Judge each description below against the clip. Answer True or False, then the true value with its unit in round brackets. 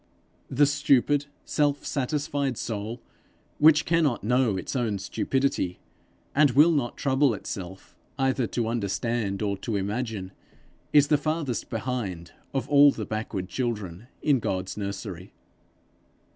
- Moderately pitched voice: False (120 Hz)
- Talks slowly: True (125 wpm)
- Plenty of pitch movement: True (5.8 semitones)